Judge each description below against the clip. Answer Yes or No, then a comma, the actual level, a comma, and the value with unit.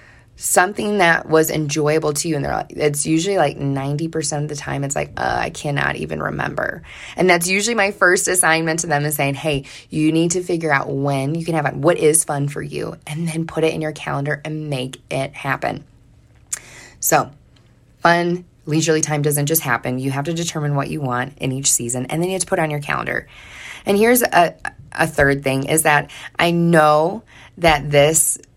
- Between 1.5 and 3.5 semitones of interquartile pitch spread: Yes, average, 2.8 semitones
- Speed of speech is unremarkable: No, fast, 210 wpm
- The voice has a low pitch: No, medium, 150 Hz